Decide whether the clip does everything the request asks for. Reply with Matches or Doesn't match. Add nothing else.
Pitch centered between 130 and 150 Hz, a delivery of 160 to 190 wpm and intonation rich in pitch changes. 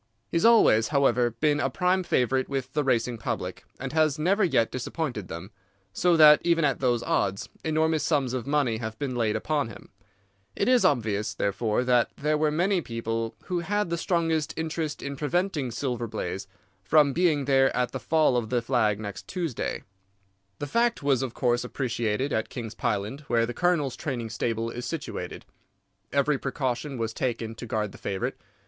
Doesn't match